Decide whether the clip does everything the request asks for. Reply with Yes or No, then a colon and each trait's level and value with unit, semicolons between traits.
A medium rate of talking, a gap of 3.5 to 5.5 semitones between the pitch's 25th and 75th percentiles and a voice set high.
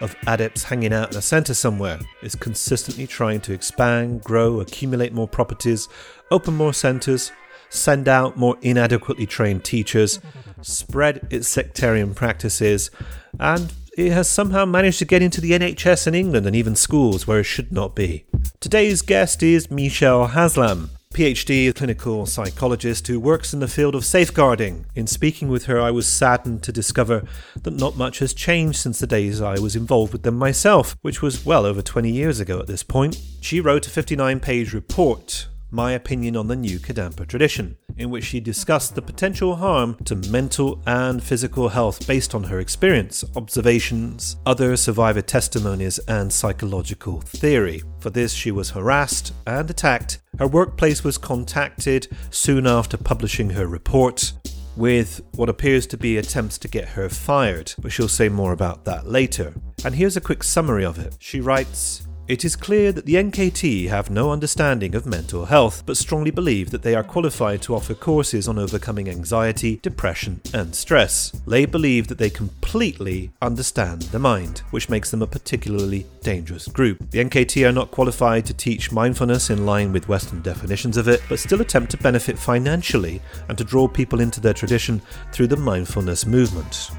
No: average, 175 wpm; average, 4.5 semitones; low, 120 Hz